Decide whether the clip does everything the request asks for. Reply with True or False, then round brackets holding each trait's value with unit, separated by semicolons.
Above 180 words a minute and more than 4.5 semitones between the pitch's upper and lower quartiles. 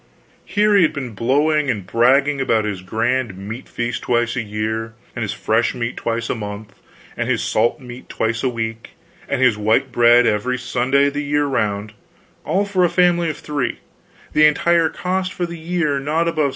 True (190 wpm; 5.1 semitones)